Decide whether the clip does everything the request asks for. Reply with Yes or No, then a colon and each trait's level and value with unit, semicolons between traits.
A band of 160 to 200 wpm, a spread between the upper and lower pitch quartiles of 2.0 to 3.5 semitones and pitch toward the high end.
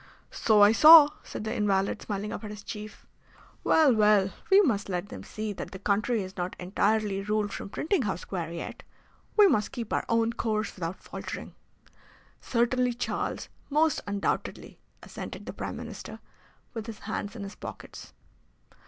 Yes: average, 165 wpm; average, 2.8 semitones; high, 210 Hz